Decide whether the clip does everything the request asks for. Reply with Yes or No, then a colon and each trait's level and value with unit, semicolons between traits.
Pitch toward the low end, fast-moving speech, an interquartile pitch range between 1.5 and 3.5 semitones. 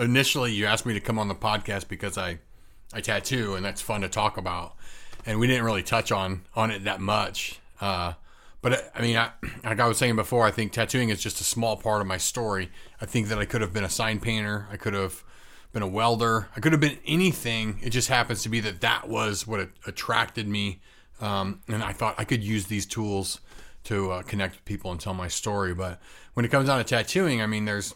Yes: low, 110 Hz; fast, 240 wpm; average, 2.8 semitones